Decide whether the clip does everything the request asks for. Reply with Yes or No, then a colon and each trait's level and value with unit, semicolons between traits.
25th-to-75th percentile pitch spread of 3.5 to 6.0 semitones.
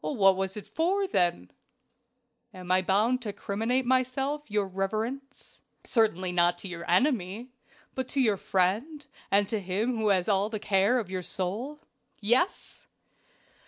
Yes: average, 5.1 semitones